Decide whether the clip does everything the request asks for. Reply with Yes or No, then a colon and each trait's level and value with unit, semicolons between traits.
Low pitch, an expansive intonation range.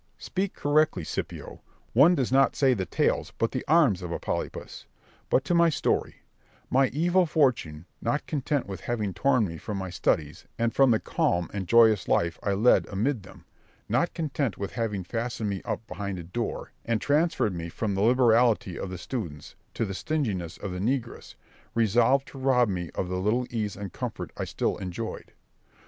Yes: low, 115 Hz; wide, 6.0 semitones